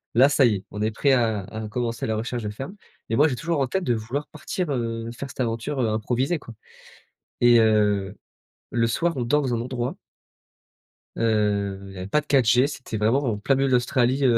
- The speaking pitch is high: No, low, 120 Hz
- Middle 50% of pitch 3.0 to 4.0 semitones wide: Yes, average, 3.6 semitones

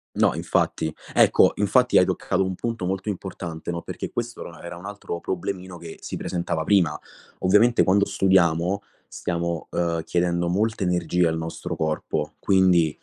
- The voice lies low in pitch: Yes, very low, 90 Hz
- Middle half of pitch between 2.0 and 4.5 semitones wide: Yes, narrow, 2.4 semitones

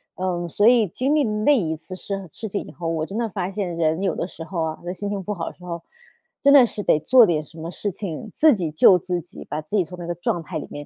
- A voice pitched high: No, medium, 180 Hz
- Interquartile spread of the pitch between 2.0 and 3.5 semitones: No, average, 3.9 semitones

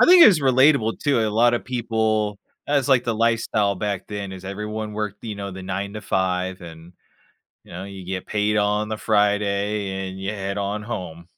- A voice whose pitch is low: Yes, low, 105 Hz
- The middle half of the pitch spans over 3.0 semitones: No, narrow, 2.5 semitones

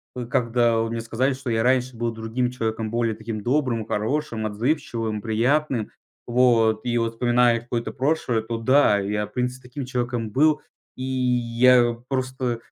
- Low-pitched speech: Yes, low, 120 Hz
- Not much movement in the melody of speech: Yes, narrow, 2.1 semitones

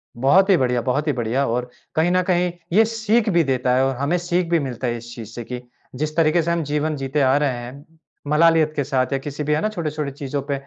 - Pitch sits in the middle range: Yes, medium, 145 Hz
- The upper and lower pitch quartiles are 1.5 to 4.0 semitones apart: No, average, 4.5 semitones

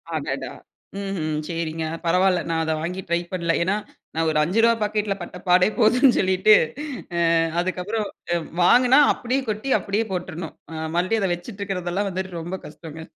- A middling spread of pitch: Yes, average, 3.6 semitones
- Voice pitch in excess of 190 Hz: No, medium, 185 Hz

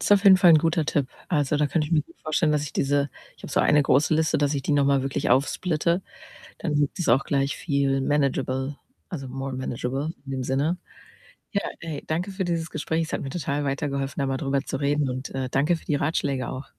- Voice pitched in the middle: Yes, medium, 145 Hz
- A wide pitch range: No, narrow, 2.6 semitones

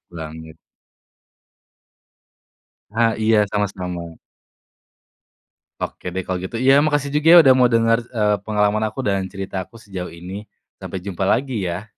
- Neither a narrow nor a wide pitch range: Yes, average, 3.9 semitones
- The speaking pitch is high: No, low, 105 Hz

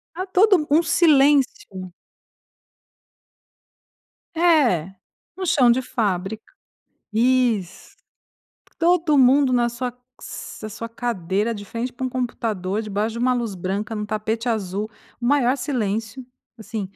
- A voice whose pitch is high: Yes, high, 235 Hz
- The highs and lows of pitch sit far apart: No, average, 3.8 semitones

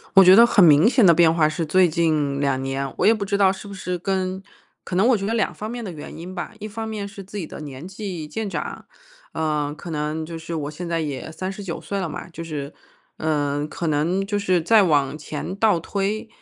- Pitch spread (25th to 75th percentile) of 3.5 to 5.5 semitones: Yes, average, 4.5 semitones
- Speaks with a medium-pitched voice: Yes, medium, 175 Hz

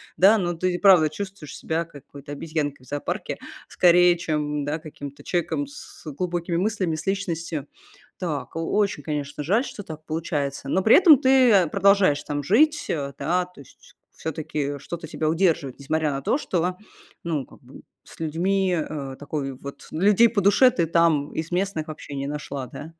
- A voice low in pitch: No, medium, 165 Hz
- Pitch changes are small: No, average, 4.4 semitones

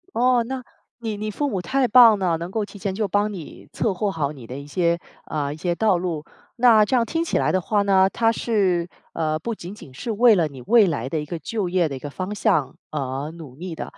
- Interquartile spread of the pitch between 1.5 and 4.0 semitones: No, wide, 5.5 semitones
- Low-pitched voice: No, medium, 185 Hz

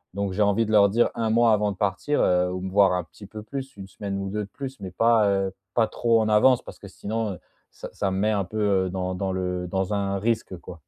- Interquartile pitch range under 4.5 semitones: Yes, narrow, 2.6 semitones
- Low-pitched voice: Yes, low, 100 Hz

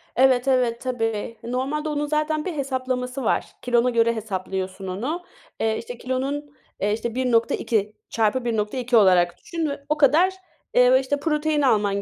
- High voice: Yes, very high, 250 Hz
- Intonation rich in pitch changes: No, average, 4.2 semitones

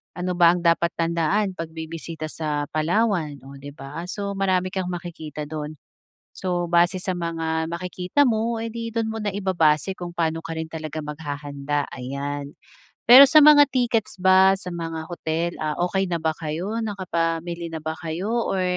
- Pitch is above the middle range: No, medium, 170 Hz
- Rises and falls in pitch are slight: No, average, 3.2 semitones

